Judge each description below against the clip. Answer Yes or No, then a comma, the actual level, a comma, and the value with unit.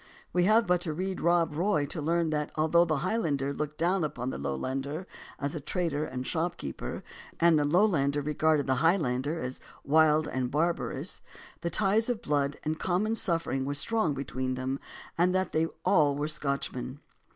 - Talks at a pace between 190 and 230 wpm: No, average, 175 wpm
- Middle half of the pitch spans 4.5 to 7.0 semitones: No, average, 3.7 semitones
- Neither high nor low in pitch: Yes, medium, 155 Hz